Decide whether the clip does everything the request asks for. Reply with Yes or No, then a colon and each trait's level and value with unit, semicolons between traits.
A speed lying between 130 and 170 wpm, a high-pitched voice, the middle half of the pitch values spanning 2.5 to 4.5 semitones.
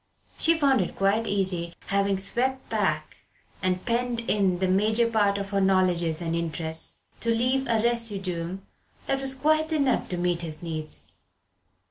No: average, 155 wpm; high, 200 Hz; average, 5.0 semitones